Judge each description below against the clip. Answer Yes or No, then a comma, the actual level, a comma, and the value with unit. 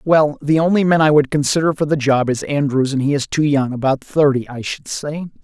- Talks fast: Yes, fast, 230 wpm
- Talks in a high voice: No, medium, 145 Hz